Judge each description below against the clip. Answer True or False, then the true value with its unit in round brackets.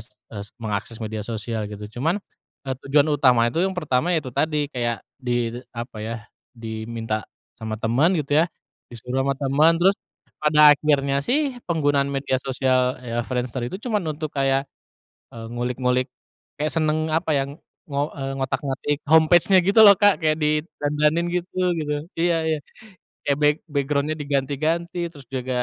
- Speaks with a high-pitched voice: False (140 Hz)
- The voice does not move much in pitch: False (3.9 semitones)